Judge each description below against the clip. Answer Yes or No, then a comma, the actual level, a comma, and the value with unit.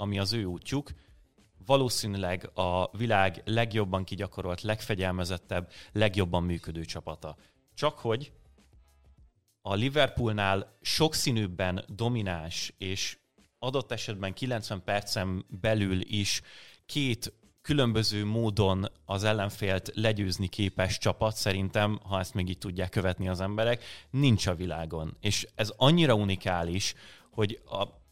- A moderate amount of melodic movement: Yes, average, 3.1 semitones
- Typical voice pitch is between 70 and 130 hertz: Yes, low, 100 Hz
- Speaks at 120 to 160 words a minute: No, average, 110 wpm